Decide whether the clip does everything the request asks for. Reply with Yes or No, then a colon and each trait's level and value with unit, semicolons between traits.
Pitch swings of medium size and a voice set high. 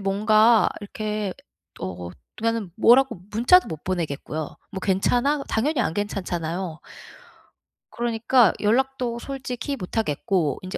Yes: average, 4.7 semitones; high, 215 Hz